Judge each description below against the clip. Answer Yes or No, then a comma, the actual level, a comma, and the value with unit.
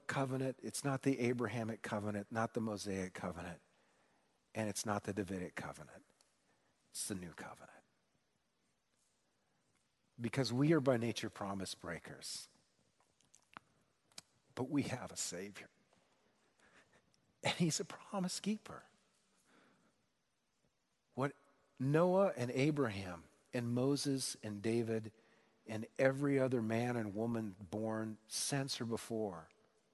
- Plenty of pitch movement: No, average, 4.3 semitones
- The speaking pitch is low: Yes, low, 115 Hz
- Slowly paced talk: Yes, slow, 110 wpm